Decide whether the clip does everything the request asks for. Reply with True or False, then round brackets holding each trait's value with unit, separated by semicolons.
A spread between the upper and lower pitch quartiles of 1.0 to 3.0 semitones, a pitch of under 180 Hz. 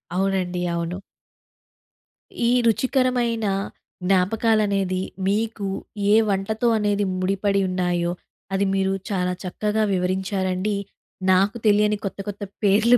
False (2.4 semitones; 195 Hz)